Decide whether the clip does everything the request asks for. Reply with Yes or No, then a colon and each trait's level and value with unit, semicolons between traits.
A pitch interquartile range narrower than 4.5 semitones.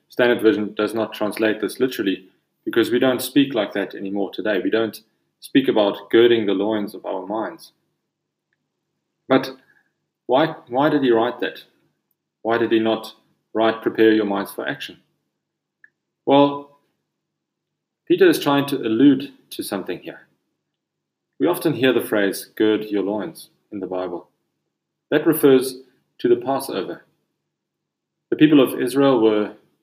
No: average, 5.0 semitones